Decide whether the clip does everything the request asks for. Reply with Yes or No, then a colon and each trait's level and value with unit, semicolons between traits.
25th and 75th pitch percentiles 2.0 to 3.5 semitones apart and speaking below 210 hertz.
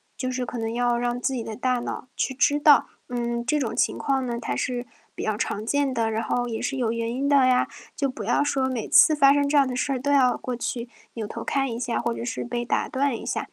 No: narrow, 2.6 semitones; high, 245 Hz